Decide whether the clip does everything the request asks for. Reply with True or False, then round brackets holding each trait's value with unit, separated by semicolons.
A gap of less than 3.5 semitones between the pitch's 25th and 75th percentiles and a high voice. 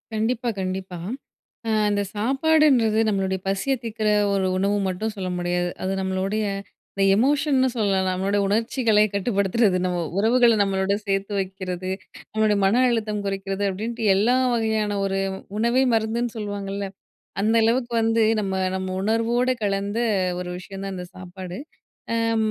True (2.9 semitones; 205 Hz)